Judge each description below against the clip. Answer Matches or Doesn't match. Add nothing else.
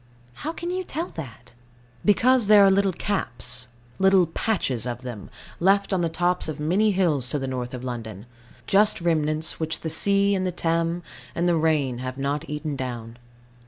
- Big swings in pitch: Matches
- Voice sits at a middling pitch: Matches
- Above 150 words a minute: Matches